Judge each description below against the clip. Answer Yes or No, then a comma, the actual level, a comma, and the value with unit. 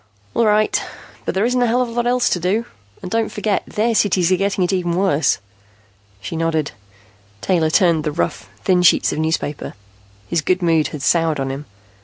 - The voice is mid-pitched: Yes, medium, 180 Hz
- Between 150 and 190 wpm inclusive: No, average, 200 wpm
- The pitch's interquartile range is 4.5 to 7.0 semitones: Yes, average, 4.9 semitones